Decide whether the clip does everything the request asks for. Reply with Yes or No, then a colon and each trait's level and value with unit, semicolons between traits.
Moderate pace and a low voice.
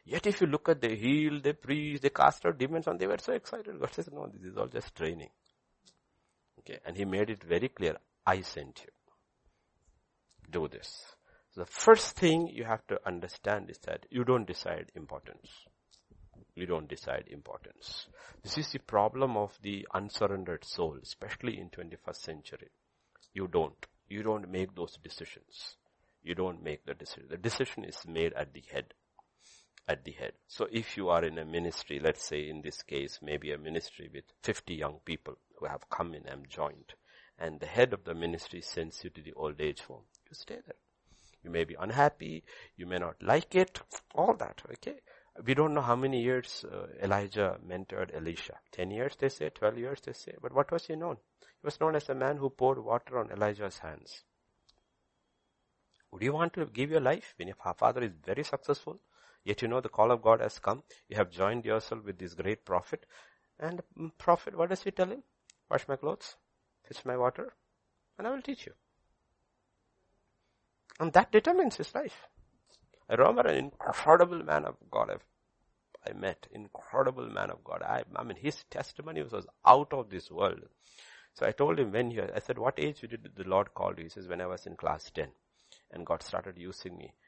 Yes: average, 195 wpm; low, 115 Hz